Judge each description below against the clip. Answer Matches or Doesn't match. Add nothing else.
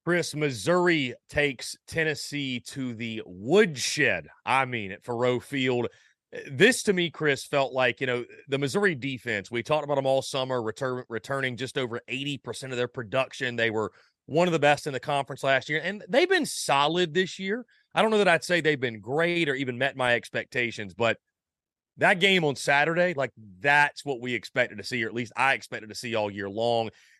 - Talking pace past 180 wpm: Matches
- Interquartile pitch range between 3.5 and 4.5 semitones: Matches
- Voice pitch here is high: Doesn't match